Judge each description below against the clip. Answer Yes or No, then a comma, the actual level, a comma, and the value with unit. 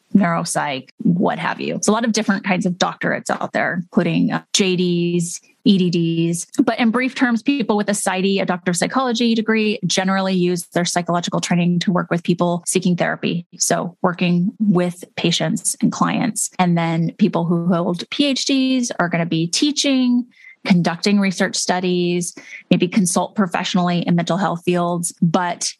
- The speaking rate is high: No, average, 160 wpm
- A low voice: No, medium, 185 Hz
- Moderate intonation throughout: Yes, average, 4.1 semitones